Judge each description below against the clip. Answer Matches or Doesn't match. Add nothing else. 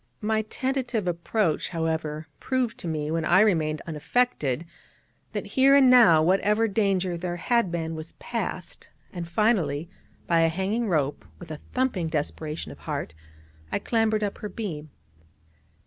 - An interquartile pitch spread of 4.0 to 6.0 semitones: Matches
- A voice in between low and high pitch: Matches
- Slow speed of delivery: Doesn't match